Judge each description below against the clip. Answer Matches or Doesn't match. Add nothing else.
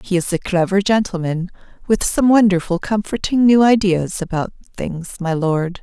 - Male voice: Doesn't match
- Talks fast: Doesn't match